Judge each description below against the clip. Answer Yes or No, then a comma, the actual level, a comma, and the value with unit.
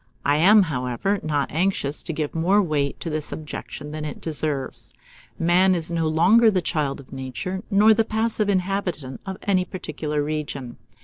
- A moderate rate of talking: Yes, average, 170 wpm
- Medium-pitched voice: Yes, medium, 160 Hz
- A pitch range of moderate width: Yes, average, 4.5 semitones